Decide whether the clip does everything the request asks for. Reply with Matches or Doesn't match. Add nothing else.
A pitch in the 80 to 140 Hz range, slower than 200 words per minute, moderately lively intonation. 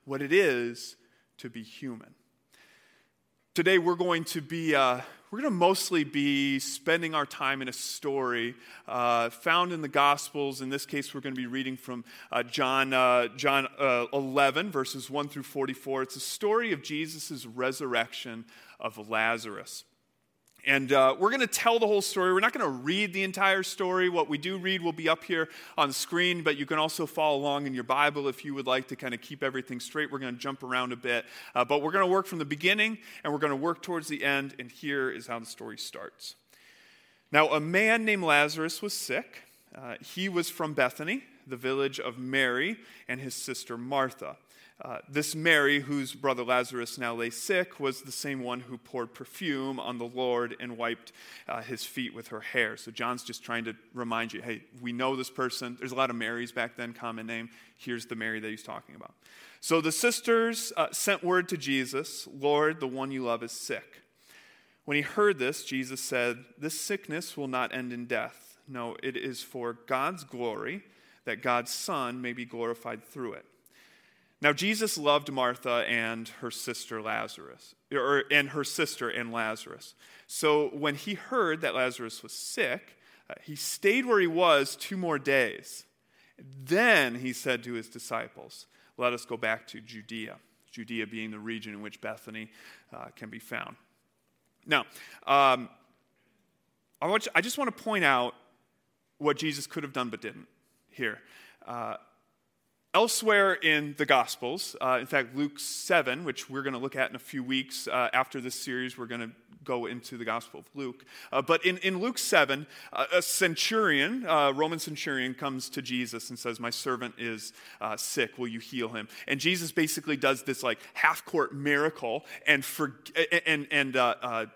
Matches